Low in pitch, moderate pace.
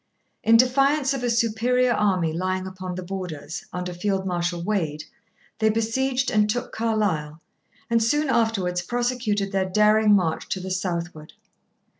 No: high, 205 Hz; average, 145 wpm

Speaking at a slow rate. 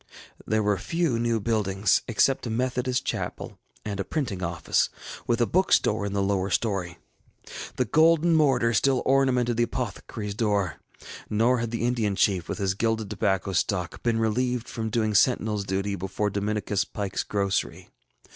No: average, 155 wpm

